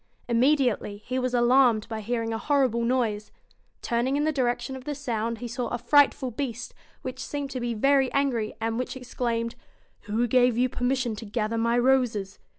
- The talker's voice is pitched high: Yes, high, 245 Hz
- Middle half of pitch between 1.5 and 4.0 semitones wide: Yes, narrow, 2.4 semitones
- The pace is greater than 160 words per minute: Yes, average, 180 wpm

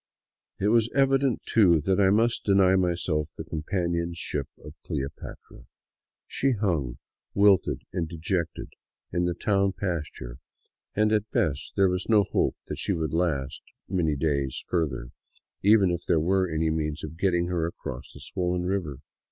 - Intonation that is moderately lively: Yes, average, 3.8 semitones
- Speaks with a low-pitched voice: Yes, very low, 90 Hz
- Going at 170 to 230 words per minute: No, average, 160 wpm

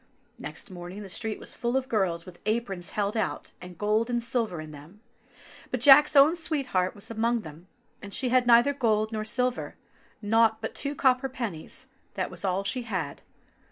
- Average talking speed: Yes, average, 190 wpm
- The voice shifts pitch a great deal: No, average, 4.6 semitones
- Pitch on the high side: Yes, high, 220 Hz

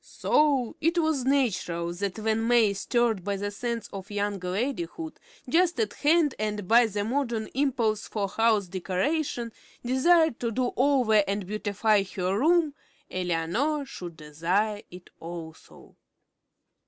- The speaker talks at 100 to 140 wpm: Yes, slow, 135 wpm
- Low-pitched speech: No, high, 220 Hz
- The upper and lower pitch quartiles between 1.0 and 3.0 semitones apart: No, wide, 5.5 semitones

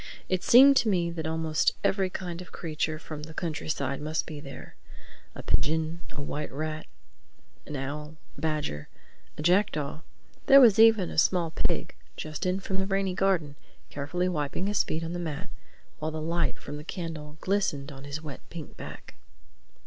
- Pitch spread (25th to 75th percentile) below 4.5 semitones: Yes, average, 3.4 semitones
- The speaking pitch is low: No, medium, 160 Hz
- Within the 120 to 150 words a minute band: No, average, 170 wpm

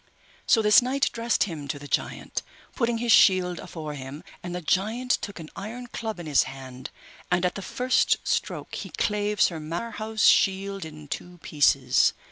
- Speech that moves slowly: No, average, 175 wpm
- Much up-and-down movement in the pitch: Yes, wide, 6.3 semitones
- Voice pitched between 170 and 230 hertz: Yes, medium, 185 Hz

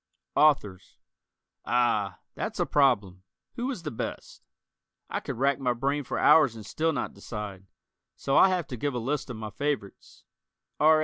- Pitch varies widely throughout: Yes, wide, 5.7 semitones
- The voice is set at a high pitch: No, low, 130 Hz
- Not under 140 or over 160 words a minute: No, average, 170 wpm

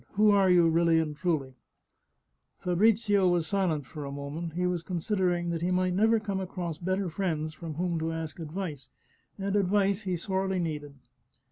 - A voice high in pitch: No, medium, 175 Hz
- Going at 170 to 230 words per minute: Yes, average, 175 wpm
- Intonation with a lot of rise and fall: No, average, 3.1 semitones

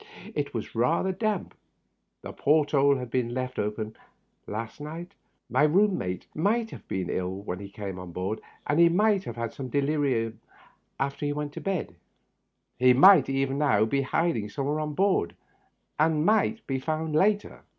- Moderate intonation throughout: No, wide, 6.4 semitones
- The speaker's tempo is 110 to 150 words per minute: No, average, 170 wpm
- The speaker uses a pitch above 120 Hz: Yes, medium, 140 Hz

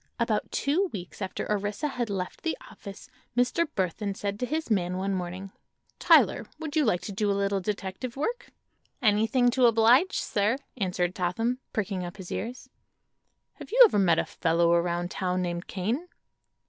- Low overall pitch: No, high, 205 Hz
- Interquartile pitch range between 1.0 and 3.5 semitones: No, average, 5.2 semitones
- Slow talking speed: No, average, 170 wpm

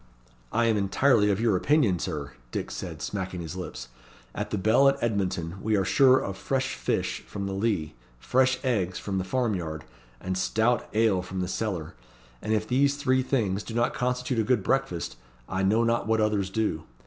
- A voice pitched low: Yes, low, 105 Hz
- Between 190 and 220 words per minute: Yes, average, 195 wpm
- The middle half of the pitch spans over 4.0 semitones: Yes, average, 4.6 semitones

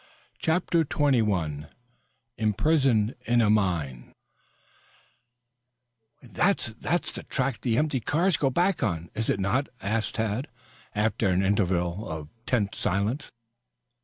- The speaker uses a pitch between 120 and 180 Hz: No, low, 110 Hz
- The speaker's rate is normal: No, slow, 120 wpm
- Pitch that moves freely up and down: Yes, wide, 6.0 semitones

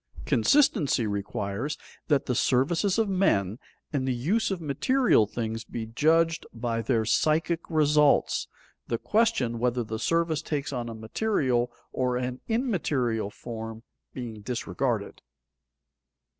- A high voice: No, low, 130 Hz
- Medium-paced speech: No, slow, 125 wpm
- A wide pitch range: Yes, wide, 6.0 semitones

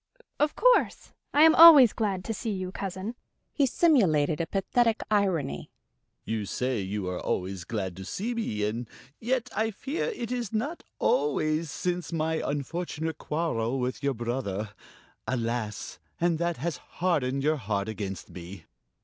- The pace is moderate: Yes, average, 150 wpm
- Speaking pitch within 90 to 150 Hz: No, medium, 160 Hz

